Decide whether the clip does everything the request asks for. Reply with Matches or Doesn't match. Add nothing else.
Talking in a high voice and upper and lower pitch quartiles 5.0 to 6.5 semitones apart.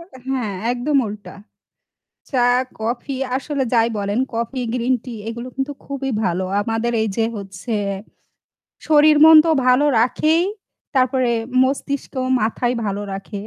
Doesn't match